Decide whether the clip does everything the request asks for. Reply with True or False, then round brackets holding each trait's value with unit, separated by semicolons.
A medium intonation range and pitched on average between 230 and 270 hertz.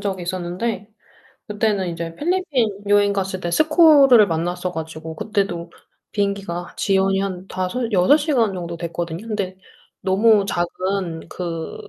False (3.5 semitones; 190 Hz)